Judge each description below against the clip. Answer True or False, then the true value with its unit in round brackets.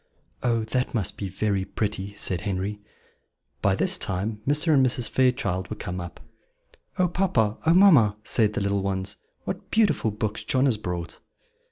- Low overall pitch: True (105 Hz)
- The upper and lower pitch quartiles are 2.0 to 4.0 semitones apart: False (4.8 semitones)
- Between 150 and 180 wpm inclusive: True (170 wpm)